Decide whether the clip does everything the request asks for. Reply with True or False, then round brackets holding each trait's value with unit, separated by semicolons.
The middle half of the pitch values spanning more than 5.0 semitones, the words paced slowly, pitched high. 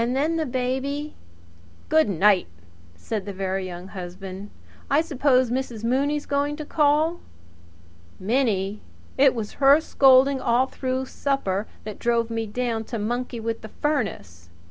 False (5.4 semitones; 145 wpm; 245 Hz)